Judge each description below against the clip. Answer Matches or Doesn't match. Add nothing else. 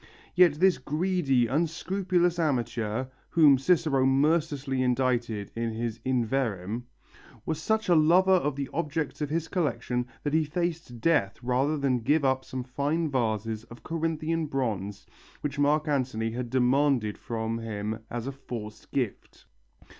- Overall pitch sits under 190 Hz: Matches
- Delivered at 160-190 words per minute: Doesn't match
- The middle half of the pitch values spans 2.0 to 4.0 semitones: Doesn't match